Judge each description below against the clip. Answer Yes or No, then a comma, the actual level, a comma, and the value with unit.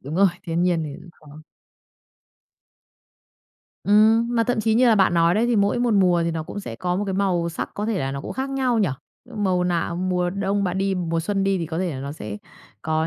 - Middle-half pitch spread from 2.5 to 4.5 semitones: Yes, average, 3.7 semitones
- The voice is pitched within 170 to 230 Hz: Yes, medium, 185 Hz